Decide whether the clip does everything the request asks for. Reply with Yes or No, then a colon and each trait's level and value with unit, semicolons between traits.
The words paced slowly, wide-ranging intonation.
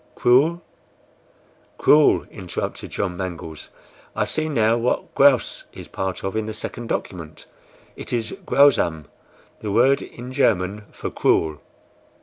Yes: slow, 130 wpm; wide, 5.9 semitones